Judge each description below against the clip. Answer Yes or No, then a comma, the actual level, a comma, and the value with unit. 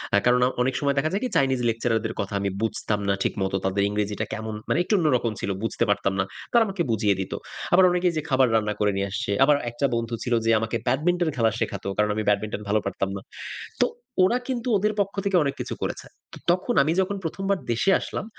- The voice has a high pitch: No, low, 120 Hz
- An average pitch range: No, wide, 8.8 semitones